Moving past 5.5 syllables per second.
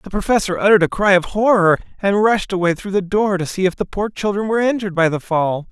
Yes: 6.3 syllables/s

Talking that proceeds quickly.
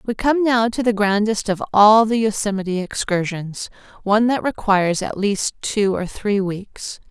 No: average, 170 wpm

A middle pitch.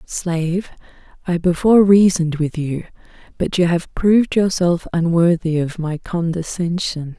Yes: medium, 175 Hz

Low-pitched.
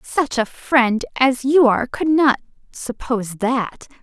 No: very high, 250 Hz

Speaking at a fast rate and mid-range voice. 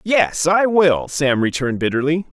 No: average, 150 wpm; medium, 155 Hz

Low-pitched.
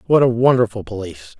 Yes: low, 120 Hz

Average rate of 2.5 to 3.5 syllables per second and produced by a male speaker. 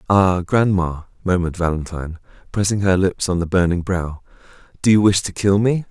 No: 5.6 syllables/s; male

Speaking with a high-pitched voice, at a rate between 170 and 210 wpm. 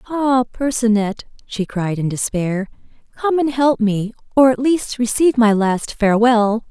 No: high, 235 Hz; average, 150 wpm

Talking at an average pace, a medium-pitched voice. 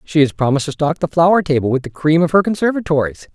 No: fast, 250 wpm; medium, 155 Hz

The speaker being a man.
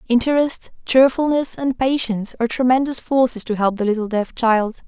No: female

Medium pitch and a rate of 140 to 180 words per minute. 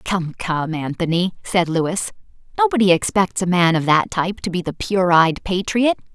Yes: medium, 180 Hz; average, 175 wpm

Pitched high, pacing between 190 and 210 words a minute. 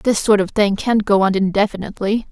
Yes: high, 205 Hz; fast, 205 wpm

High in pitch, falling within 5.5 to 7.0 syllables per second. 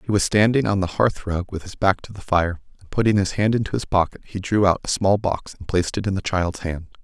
No: very low, 95 Hz; 5.9 syllables/s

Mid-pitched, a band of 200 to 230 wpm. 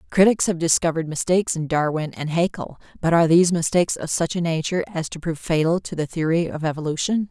Yes: medium, 165 Hz; fast, 205 wpm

